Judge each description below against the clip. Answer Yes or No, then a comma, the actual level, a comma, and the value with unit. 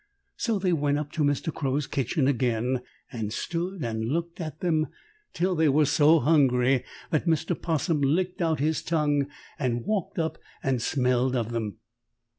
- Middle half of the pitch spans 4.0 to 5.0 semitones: Yes, average, 4.3 semitones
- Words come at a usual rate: Yes, average, 165 wpm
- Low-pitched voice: No, medium, 145 Hz